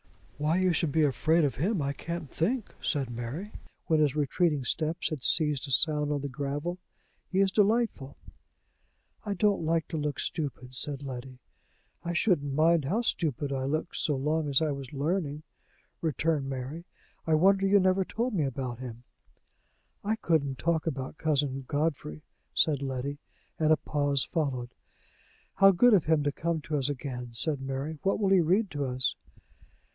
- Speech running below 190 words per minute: Yes, average, 170 wpm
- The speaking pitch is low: No, medium, 150 Hz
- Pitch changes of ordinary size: Yes, average, 3.7 semitones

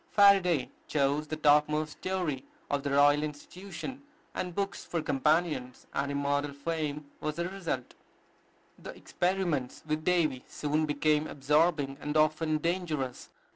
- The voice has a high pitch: No, medium, 150 Hz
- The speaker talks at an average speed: No, slow, 130 wpm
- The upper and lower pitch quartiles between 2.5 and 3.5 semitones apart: Yes, average, 3.1 semitones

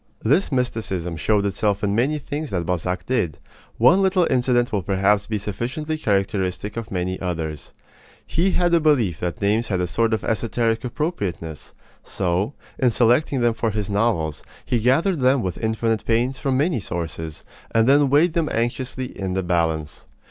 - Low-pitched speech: Yes, low, 110 Hz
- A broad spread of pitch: Yes, wide, 5.7 semitones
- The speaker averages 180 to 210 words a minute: No, average, 170 wpm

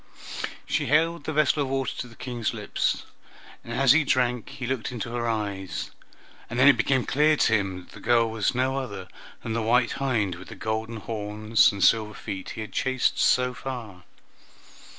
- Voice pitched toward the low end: Yes, low, 120 Hz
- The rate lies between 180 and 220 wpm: Yes, average, 190 wpm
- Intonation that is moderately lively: Yes, average, 3.3 semitones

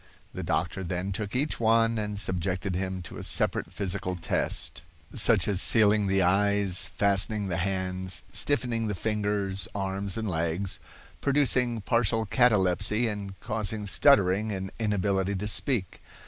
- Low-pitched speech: Yes, low, 100 Hz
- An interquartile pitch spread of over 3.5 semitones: No, narrow, 2.6 semitones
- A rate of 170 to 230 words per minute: No, average, 140 wpm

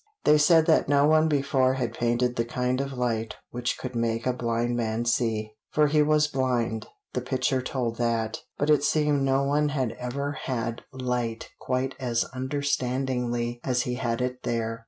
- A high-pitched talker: No, low, 125 Hz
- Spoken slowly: No, average, 175 wpm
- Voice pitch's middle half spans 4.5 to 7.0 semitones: No, average, 2.8 semitones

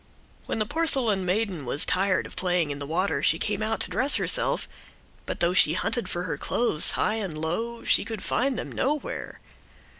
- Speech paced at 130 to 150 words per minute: No, average, 190 wpm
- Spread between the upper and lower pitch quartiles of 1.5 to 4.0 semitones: No, average, 5.2 semitones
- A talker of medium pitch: No, high, 200 Hz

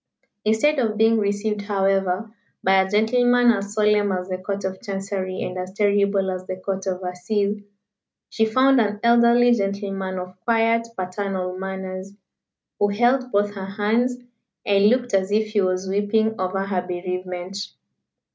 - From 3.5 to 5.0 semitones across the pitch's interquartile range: No, narrow, 2.6 semitones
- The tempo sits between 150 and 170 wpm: Yes, average, 155 wpm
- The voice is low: No, high, 200 Hz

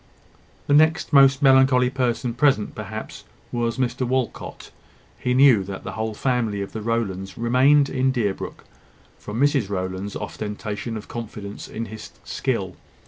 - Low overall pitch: Yes, low, 115 Hz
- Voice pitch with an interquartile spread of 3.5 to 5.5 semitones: Yes, average, 4.0 semitones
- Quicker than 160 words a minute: No, average, 140 wpm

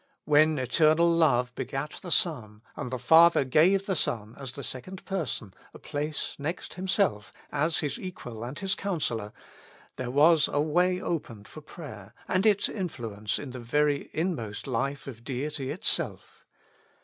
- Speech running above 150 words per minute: Yes, average, 160 wpm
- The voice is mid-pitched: Yes, medium, 145 Hz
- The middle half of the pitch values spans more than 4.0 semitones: Yes, wide, 5.5 semitones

